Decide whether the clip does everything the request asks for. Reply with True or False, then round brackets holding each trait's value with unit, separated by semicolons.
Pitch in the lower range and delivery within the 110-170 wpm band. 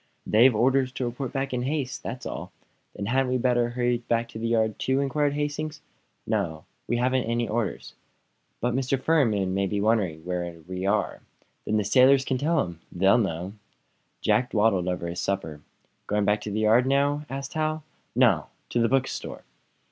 False (120 Hz; 180 wpm)